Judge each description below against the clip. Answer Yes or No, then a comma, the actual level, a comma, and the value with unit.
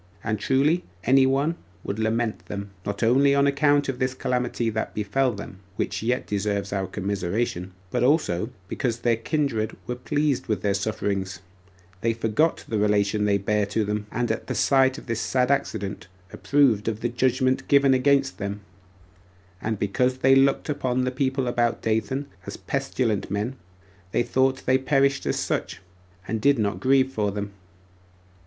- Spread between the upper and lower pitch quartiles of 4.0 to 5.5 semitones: Yes, average, 4.4 semitones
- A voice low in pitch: Yes, low, 120 Hz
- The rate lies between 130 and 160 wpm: No, average, 170 wpm